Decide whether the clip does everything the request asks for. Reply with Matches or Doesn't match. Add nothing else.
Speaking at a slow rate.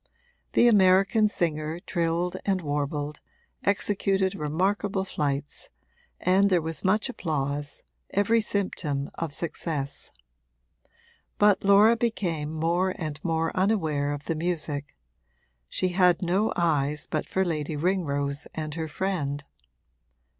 Matches